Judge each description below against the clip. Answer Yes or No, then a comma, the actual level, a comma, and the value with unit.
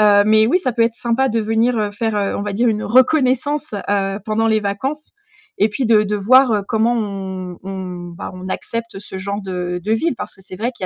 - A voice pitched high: Yes, high, 215 Hz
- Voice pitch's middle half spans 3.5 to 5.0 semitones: No, average, 2.9 semitones